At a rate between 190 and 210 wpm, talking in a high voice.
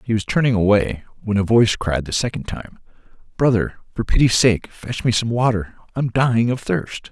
No: average, 195 wpm; low, 110 Hz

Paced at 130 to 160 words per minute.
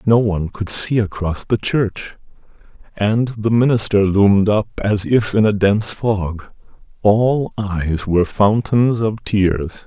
Yes: average, 145 wpm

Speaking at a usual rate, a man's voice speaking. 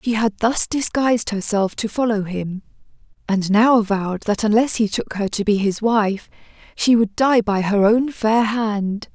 No: average, 185 wpm; female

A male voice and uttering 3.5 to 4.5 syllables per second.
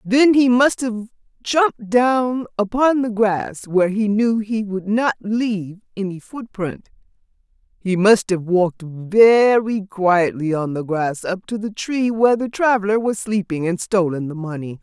No: female; 4.2 syllables/s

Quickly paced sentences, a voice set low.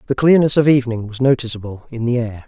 Yes: fast, 220 wpm; low, 125 Hz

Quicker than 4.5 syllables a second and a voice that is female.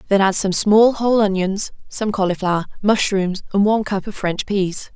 Yes: 5.1 syllables/s; female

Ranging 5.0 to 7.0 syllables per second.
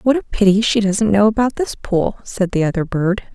Yes: 5.2 syllables/s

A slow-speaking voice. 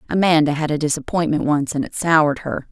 No: average, 200 wpm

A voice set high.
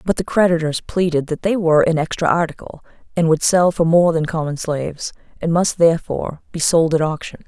No: medium, 165 Hz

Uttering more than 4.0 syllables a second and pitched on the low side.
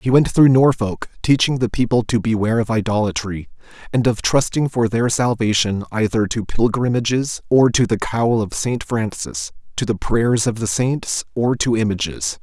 Yes: 4.8 syllables/s; low, 115 Hz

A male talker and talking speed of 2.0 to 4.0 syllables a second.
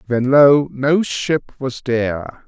Yes: male; 3.3 syllables/s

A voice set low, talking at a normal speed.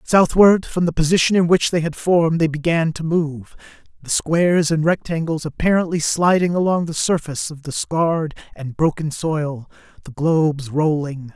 No: medium, 160 Hz; average, 165 wpm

